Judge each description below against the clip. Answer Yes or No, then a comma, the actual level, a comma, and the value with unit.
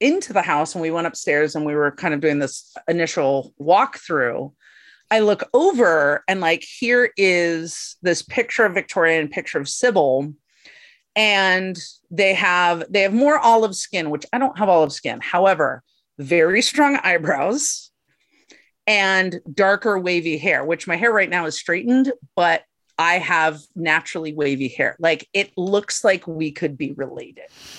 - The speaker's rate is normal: Yes, average, 160 wpm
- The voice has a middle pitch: Yes, medium, 175 Hz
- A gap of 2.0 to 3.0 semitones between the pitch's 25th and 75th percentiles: No, average, 4.6 semitones